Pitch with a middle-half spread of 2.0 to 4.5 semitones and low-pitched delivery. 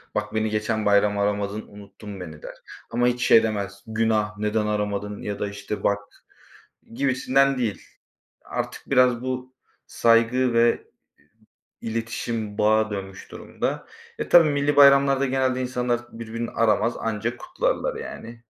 Yes: average, 3.4 semitones; low, 115 Hz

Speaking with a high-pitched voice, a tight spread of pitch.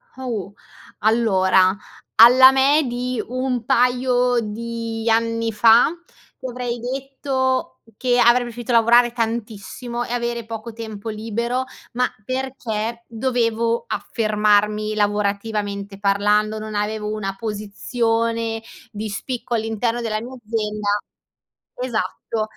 Yes: high, 230 Hz; narrow, 2.3 semitones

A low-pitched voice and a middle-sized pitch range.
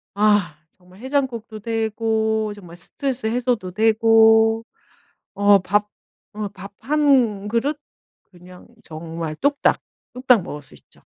No: high, 220 Hz; average, 3.3 semitones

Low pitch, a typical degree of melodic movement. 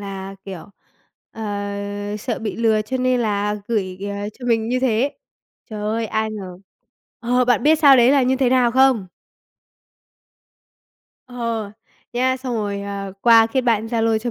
No: high, 225 Hz; average, 3.3 semitones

